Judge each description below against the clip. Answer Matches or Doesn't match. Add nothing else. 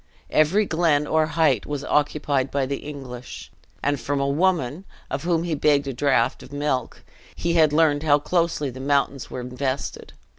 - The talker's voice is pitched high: Doesn't match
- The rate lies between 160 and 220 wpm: Matches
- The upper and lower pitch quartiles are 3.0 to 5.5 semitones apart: Doesn't match